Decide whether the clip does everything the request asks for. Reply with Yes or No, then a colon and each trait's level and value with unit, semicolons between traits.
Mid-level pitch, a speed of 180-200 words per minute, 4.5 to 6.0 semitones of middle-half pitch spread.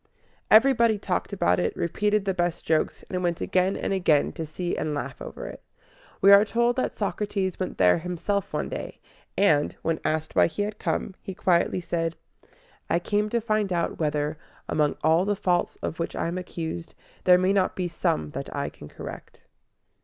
No: medium, 180 Hz; average, 190 wpm; average, 3.8 semitones